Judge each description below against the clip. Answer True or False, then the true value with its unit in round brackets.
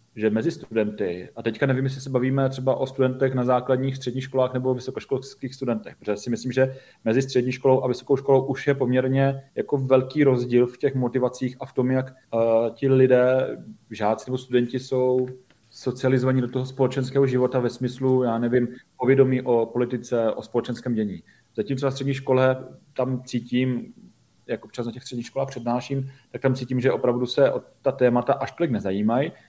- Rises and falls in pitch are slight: True (1.4 semitones)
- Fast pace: True (180 wpm)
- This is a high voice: False (130 Hz)